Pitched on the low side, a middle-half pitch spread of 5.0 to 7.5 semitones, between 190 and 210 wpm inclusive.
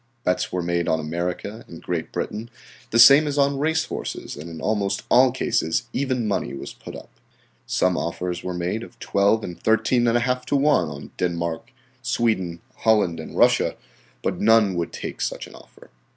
No: low, 100 Hz; wide, 5.6 semitones; average, 175 wpm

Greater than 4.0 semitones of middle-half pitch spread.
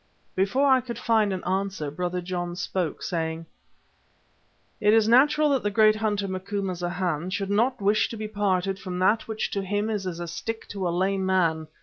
No: average, 3.1 semitones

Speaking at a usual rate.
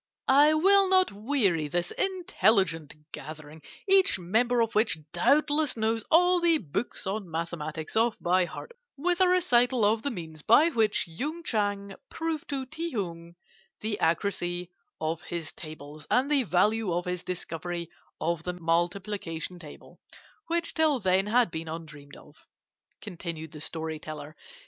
Yes: average, 150 wpm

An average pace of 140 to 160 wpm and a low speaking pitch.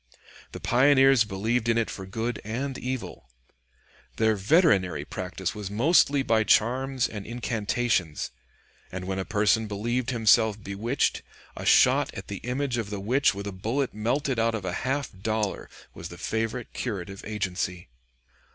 Yes: average, 150 wpm; low, 110 Hz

